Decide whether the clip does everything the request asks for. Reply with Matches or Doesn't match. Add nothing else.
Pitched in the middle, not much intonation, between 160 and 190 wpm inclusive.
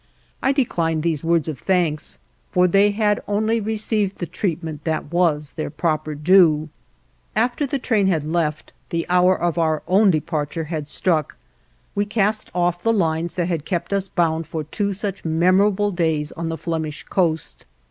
Doesn't match